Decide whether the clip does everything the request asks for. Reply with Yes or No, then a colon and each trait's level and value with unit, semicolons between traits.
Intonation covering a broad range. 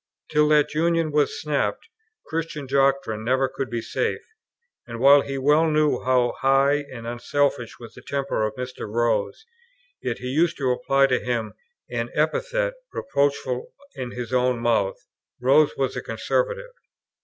No: average, 3.5 semitones